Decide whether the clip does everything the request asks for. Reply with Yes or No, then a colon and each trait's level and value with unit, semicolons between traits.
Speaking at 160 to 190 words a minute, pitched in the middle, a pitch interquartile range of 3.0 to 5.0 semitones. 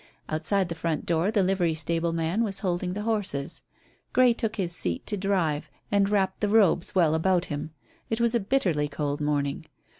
Yes: average, 185 wpm; medium, 180 Hz; average, 4.3 semitones